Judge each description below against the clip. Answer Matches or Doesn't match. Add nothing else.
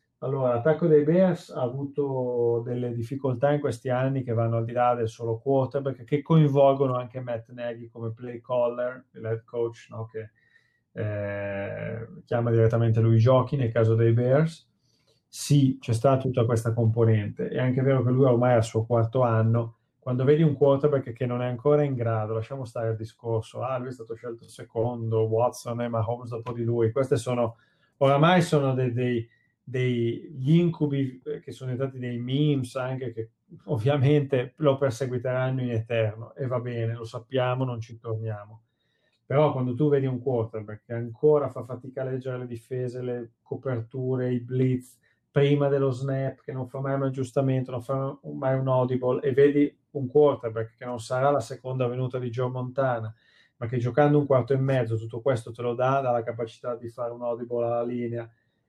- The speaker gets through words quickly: Matches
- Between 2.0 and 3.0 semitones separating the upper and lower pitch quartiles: Matches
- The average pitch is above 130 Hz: Doesn't match